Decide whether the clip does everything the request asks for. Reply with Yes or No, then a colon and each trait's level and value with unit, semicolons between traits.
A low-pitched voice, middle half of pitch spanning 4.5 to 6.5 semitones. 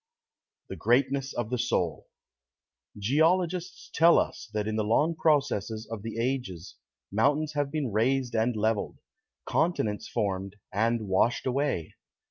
Yes: low, 120 Hz; average, 5.1 semitones